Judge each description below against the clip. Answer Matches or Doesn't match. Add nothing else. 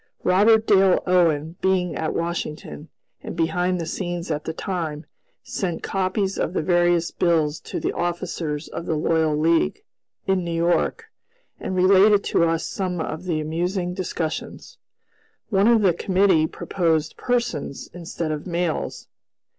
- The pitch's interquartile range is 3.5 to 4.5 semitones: Doesn't match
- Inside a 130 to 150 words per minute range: Matches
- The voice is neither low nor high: Matches